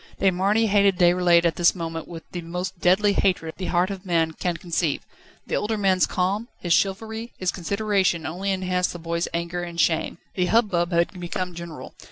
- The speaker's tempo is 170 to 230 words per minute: Yes, average, 190 wpm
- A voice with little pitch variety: Yes, narrow, 2.3 semitones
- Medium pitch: Yes, medium, 180 Hz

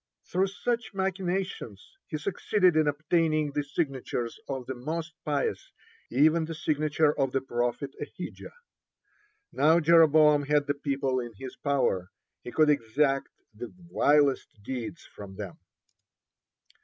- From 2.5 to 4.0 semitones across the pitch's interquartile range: Yes, average, 3.4 semitones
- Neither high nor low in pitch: Yes, medium, 145 Hz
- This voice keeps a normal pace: No, slow, 130 wpm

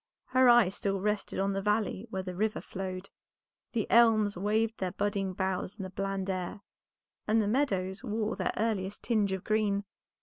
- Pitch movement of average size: No, narrow, 2.3 semitones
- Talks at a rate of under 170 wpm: No, average, 175 wpm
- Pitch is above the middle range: Yes, high, 205 Hz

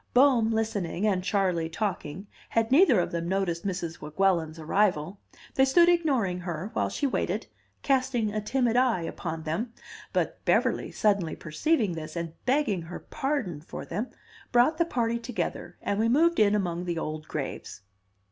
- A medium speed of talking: Yes, average, 160 wpm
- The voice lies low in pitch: No, high, 200 Hz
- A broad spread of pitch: Yes, wide, 6.4 semitones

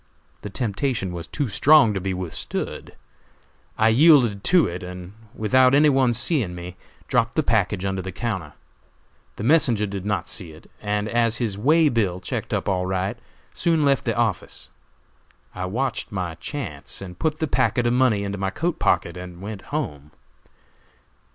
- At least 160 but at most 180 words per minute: Yes, average, 170 wpm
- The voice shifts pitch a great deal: Yes, wide, 5.7 semitones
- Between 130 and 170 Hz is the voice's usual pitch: No, low, 105 Hz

